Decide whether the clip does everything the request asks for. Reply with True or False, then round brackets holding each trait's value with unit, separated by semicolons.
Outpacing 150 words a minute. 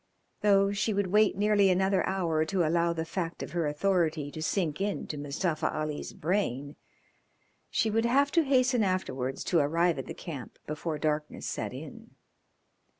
True (160 wpm)